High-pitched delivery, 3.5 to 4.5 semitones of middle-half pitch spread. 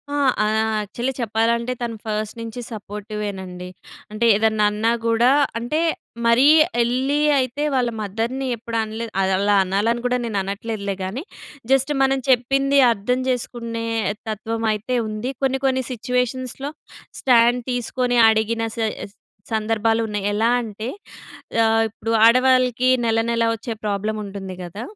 No: high, 230 Hz; average, 2.7 semitones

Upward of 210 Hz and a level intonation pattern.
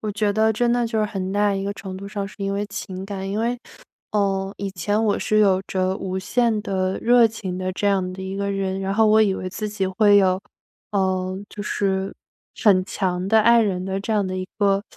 No: high, 200 Hz; narrow, 1.9 semitones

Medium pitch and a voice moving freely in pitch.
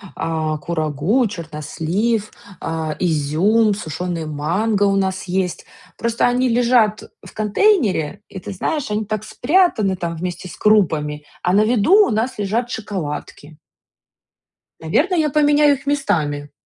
No: high, 200 Hz; wide, 6.4 semitones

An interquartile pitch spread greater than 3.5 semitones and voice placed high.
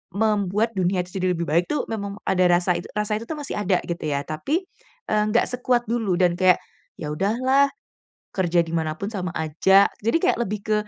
Yes: average, 4.1 semitones; high, 195 Hz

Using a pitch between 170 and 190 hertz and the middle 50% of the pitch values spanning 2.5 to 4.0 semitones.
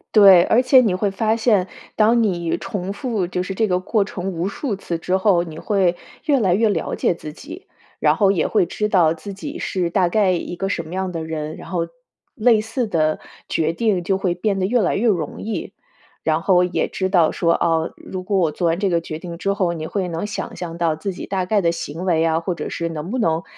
Yes: medium, 185 Hz; average, 3.5 semitones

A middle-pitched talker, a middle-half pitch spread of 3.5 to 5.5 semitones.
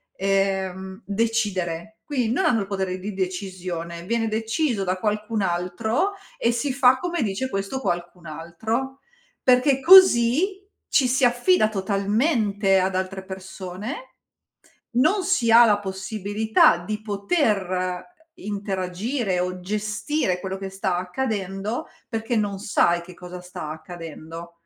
No: high, 200 Hz; average, 4.1 semitones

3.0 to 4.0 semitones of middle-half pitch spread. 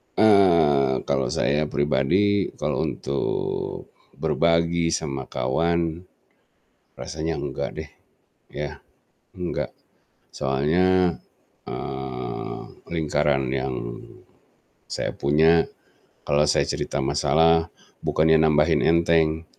Yes: average, 3.3 semitones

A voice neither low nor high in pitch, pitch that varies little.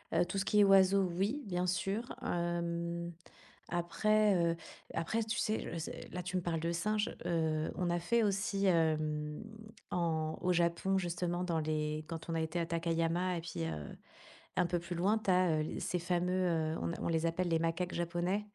Yes: medium, 175 Hz; narrow, 2.2 semitones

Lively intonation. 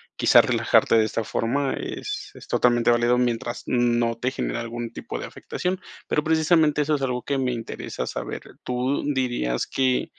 No: average, 2.7 semitones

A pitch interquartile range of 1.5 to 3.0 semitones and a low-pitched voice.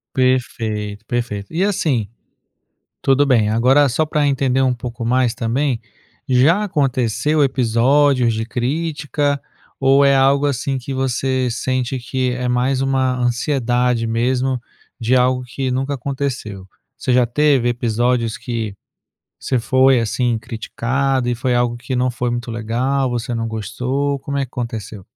Yes: narrow, 2.4 semitones; low, 125 Hz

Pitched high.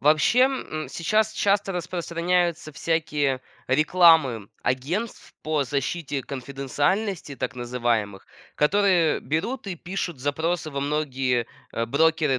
No: medium, 155 Hz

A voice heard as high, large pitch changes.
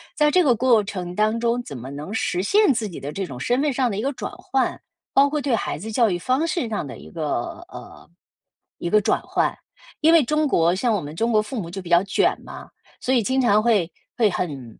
Yes: high, 215 Hz; wide, 6.6 semitones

